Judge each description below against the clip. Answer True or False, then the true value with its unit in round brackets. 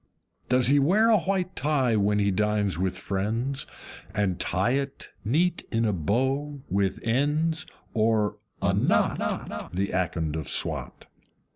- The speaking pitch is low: True (115 Hz)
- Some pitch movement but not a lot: False (6.3 semitones)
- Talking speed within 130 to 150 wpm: True (140 wpm)